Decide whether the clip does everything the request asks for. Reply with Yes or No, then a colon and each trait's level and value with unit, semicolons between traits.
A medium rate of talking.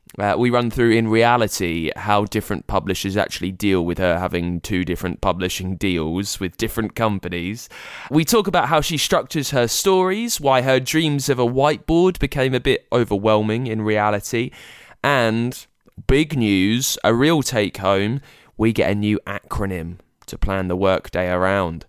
Yes: average, 160 wpm